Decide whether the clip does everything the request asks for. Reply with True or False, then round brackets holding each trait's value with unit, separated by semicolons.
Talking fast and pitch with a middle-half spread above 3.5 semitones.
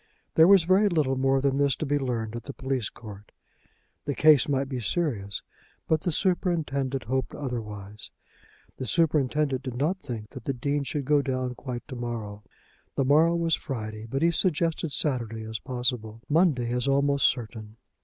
False (175 wpm; 4.1 semitones)